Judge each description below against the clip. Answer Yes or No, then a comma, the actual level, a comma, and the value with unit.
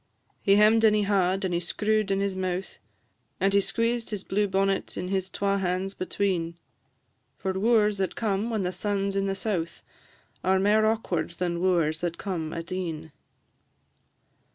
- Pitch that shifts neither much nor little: No, narrow, 2.2 semitones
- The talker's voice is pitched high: Yes, high, 195 Hz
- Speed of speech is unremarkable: Yes, average, 170 wpm